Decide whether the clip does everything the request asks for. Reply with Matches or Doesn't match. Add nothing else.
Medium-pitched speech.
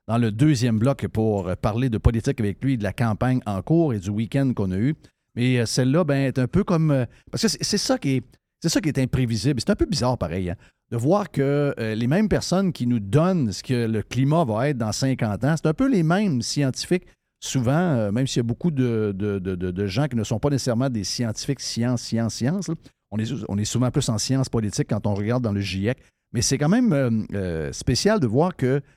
Doesn't match